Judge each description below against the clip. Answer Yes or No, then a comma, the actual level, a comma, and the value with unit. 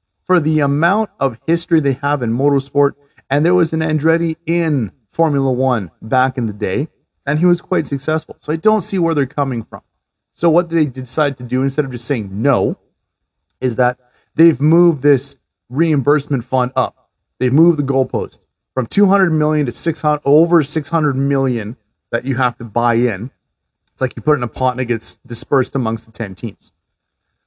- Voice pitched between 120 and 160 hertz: Yes, medium, 140 Hz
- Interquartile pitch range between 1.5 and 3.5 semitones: No, average, 4.3 semitones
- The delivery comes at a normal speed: Yes, average, 195 wpm